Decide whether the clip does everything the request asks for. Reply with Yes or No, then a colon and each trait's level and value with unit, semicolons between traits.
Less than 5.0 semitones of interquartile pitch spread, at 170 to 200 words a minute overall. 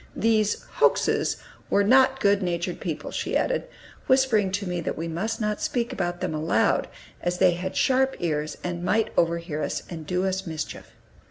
Yes: average, 4.2 semitones; average, 175 wpm